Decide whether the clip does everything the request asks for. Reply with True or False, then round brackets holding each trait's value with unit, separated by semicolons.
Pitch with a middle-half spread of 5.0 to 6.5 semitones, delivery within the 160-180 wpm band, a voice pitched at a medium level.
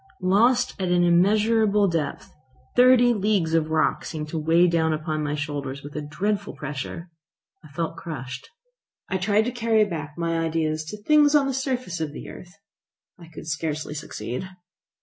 True (5.3 semitones; 165 wpm; 170 Hz)